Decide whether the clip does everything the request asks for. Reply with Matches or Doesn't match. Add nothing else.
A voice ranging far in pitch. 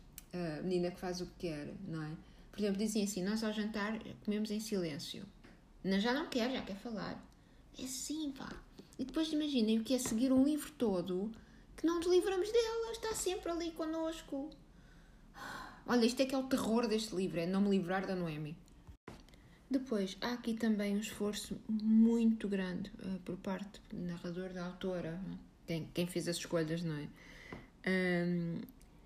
Matches